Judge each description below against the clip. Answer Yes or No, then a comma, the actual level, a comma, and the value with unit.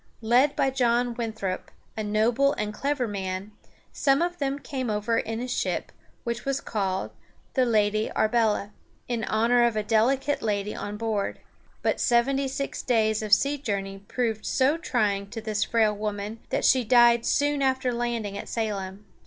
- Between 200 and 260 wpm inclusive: No, average, 165 wpm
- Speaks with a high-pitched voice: Yes, high, 230 Hz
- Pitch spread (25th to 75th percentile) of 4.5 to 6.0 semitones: No, average, 3.5 semitones